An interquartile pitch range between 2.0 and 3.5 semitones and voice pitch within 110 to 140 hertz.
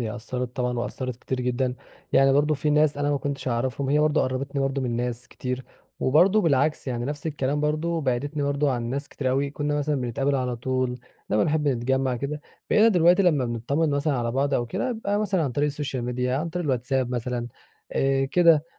Yes: average, 3.0 semitones; low, 135 Hz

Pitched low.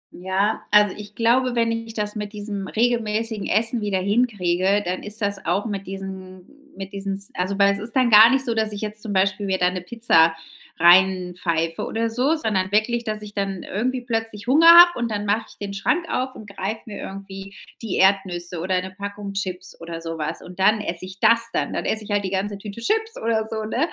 No: high, 205 Hz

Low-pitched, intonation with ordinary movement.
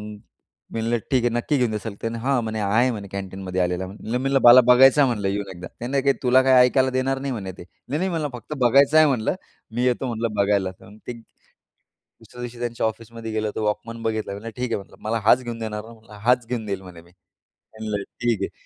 Yes: low, 115 Hz; average, 3.1 semitones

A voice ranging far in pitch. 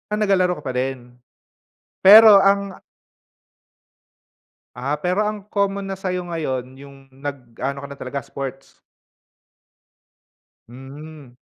Yes: wide, 6.7 semitones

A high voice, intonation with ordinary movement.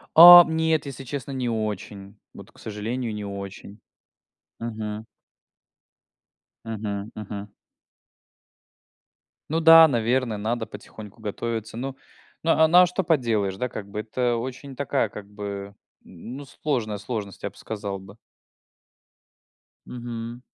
No: low, 115 Hz; average, 4.2 semitones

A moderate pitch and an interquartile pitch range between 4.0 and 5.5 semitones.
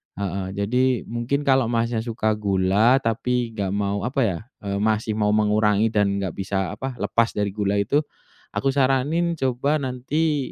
No: low, 115 Hz; average, 4.3 semitones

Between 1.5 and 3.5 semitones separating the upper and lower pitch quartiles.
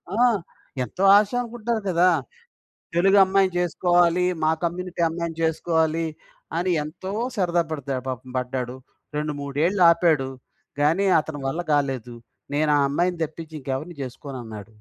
No: average, 4.1 semitones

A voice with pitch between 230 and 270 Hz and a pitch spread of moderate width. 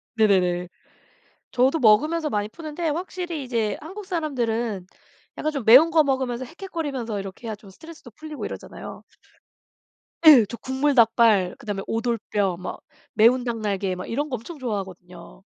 No: high, 240 Hz; wide, 6.4 semitones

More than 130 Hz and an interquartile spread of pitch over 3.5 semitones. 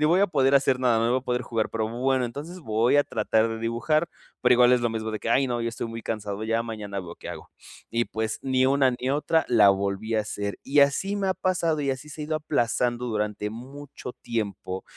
No: low, 120 Hz; average, 3.9 semitones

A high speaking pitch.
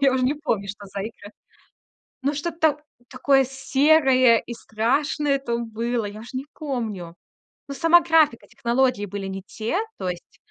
Yes: very high, 250 Hz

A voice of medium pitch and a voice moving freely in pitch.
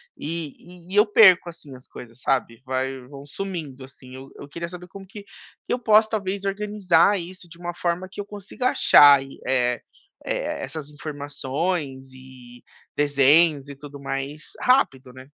Yes: medium, 150 Hz; wide, 5.7 semitones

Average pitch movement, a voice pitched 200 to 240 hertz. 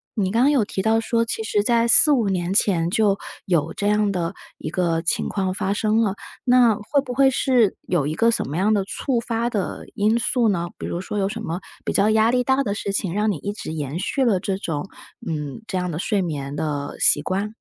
Yes: average, 4.3 semitones; high, 205 Hz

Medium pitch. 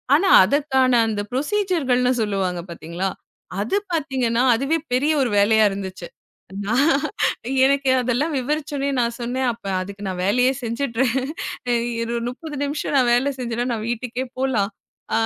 No: high, 245 Hz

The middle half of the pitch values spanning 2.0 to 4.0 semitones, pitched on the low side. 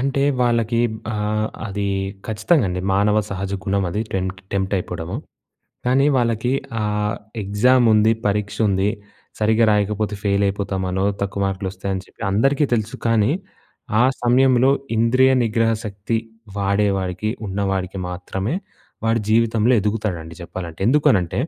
Yes: average, 2.9 semitones; low, 105 Hz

